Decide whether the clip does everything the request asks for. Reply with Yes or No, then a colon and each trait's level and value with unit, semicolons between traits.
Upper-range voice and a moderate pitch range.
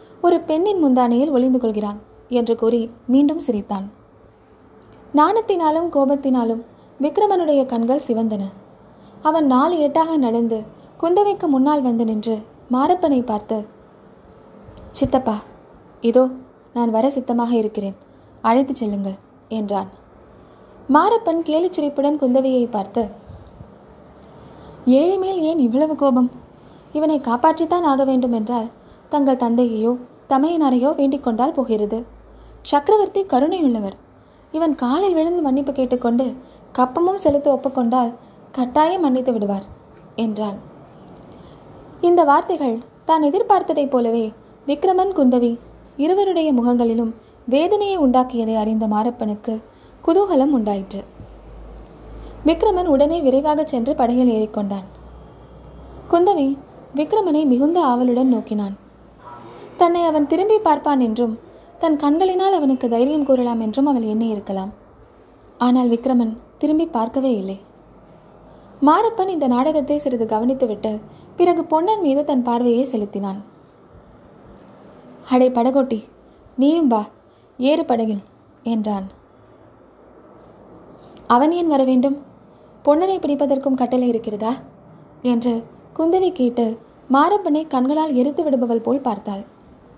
Yes: very high, 260 Hz; average, 4.8 semitones